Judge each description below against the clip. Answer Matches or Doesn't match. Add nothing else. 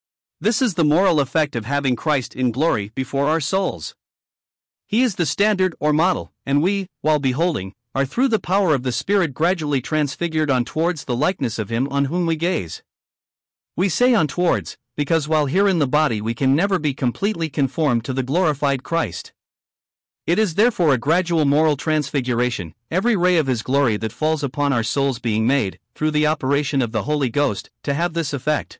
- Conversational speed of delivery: Matches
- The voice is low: Doesn't match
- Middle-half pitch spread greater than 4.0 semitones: Matches